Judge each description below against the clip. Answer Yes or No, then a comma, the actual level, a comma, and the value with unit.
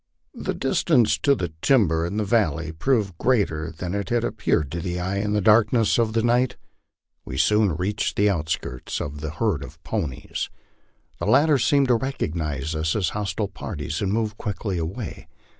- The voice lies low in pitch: Yes, low, 100 Hz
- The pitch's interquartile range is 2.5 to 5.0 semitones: No, wide, 5.6 semitones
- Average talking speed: Yes, average, 180 wpm